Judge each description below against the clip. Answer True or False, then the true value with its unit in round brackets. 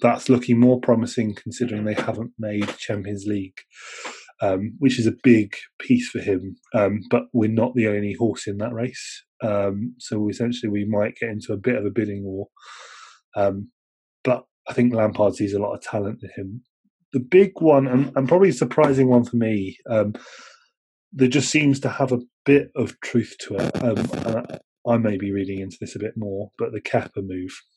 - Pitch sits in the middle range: False (115 Hz)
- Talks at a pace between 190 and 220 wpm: True (200 wpm)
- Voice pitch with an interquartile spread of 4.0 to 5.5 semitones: False (3.6 semitones)